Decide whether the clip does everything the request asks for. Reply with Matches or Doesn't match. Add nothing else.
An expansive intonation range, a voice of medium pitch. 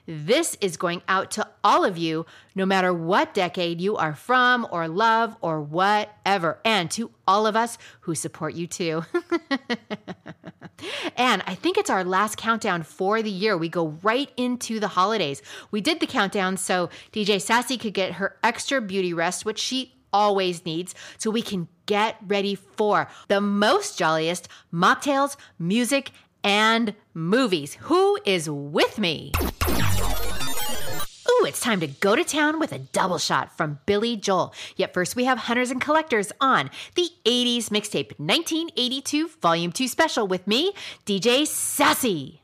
Doesn't match